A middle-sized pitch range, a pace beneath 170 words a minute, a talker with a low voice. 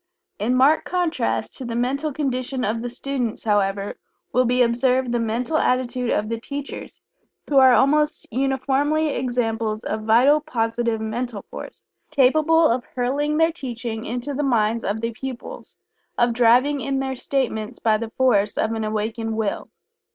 No: average, 3.3 semitones; average, 160 wpm; high, 245 Hz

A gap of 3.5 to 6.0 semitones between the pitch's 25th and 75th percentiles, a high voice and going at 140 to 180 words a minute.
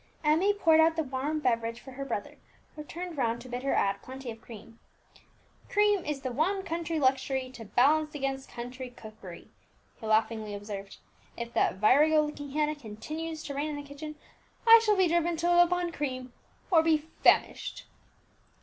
Yes: average, 5.0 semitones; very high, 285 Hz; average, 175 wpm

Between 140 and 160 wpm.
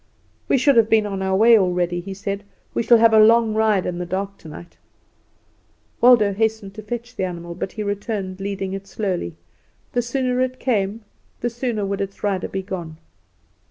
No: average, 190 wpm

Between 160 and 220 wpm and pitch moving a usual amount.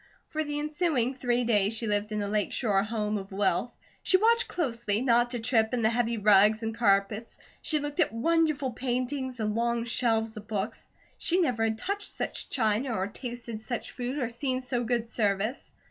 Yes: average, 190 wpm; average, 3.3 semitones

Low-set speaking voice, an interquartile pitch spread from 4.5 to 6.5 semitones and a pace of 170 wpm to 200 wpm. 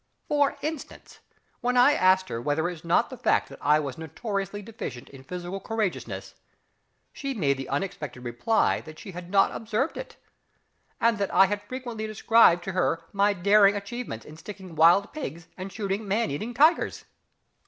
No: high, 195 Hz; average, 5.2 semitones; average, 175 wpm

